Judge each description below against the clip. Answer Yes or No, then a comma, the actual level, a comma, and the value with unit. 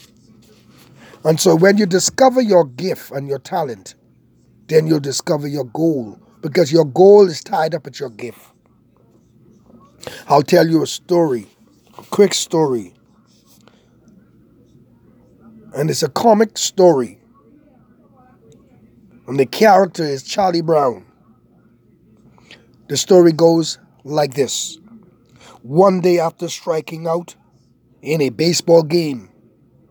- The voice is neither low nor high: Yes, medium, 165 Hz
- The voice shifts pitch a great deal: No, average, 4.6 semitones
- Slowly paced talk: Yes, slow, 115 wpm